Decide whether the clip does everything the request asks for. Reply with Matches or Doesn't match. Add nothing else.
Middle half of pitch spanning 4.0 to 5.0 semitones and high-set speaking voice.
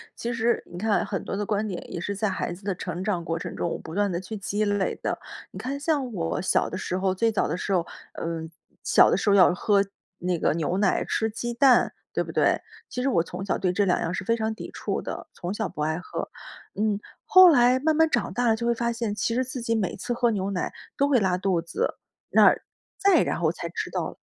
Matches